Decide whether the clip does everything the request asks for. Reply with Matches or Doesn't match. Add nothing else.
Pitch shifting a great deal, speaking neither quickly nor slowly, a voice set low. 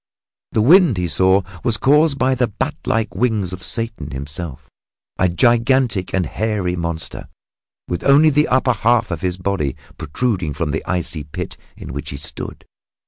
Matches